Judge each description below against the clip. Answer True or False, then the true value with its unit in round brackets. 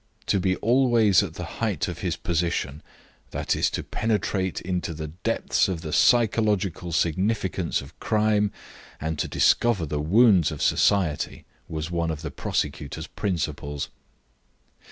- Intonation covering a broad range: False (4.9 semitones)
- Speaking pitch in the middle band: False (90 Hz)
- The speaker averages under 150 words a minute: True (135 wpm)